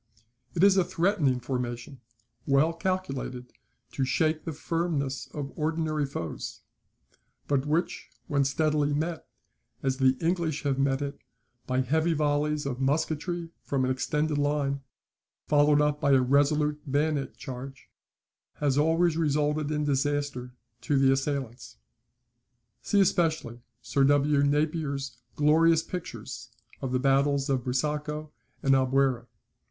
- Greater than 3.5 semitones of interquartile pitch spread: No, narrow, 2.4 semitones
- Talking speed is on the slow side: Yes, slow, 125 wpm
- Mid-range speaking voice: Yes, medium, 145 Hz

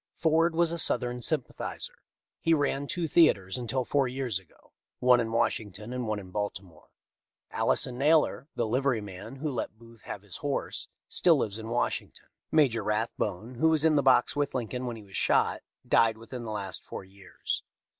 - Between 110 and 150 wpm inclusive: No, average, 180 wpm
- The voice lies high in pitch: No, low, 120 Hz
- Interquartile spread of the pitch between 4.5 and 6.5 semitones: Yes, average, 4.9 semitones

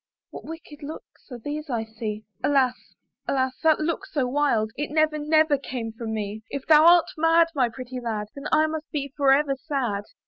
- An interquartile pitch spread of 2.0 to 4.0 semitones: No, average, 4.5 semitones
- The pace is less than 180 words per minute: No, average, 195 wpm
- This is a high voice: Yes, very high, 280 Hz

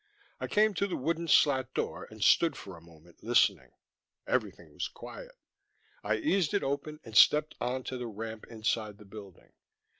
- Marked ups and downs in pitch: Yes, wide, 6.9 semitones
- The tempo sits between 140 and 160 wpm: No, average, 175 wpm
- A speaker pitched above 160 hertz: No, low, 125 Hz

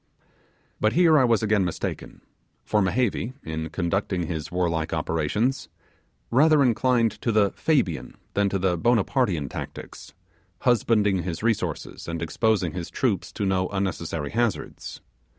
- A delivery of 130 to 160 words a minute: Yes, slow, 135 wpm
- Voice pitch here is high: No, low, 100 Hz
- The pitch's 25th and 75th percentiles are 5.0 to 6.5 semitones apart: Yes, wide, 5.4 semitones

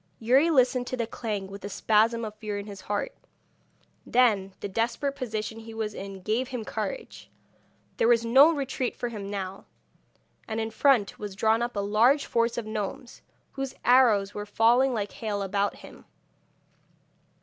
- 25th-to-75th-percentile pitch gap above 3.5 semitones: No, average, 3.2 semitones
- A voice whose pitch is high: Yes, high, 225 Hz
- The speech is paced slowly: No, average, 170 wpm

